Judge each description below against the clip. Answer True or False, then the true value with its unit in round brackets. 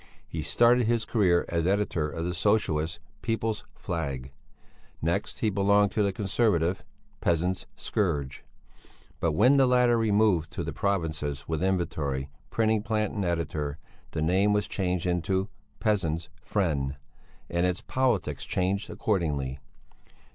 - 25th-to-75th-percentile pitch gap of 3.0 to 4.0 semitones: False (4.5 semitones)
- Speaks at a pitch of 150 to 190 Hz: False (90 Hz)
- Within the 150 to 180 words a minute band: False (135 wpm)